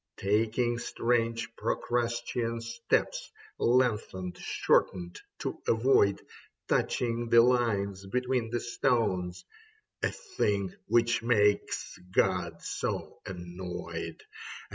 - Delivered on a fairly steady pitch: No, average, 3.2 semitones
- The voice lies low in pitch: Yes, low, 115 Hz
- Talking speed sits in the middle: No, slow, 90 wpm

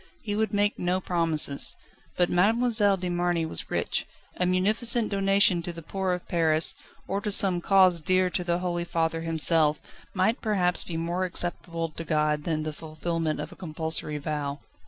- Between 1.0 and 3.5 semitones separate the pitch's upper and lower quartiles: Yes, average, 2.8 semitones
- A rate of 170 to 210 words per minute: Yes, average, 175 wpm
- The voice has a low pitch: No, medium, 175 Hz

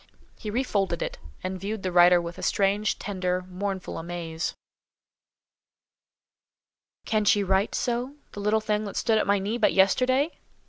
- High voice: Yes, high, 200 Hz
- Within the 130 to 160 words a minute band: Yes, average, 150 wpm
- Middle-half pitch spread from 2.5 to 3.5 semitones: Yes, average, 2.9 semitones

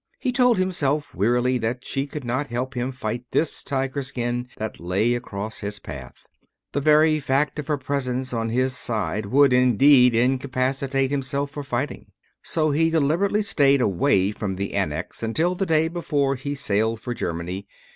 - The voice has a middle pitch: No, low, 130 Hz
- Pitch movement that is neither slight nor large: Yes, average, 3.4 semitones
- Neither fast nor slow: Yes, average, 165 wpm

